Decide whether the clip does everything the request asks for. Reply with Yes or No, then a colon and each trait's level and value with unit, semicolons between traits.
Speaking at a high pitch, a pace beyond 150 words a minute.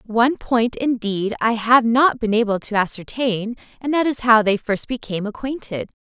Yes: high, 230 Hz; average, 180 wpm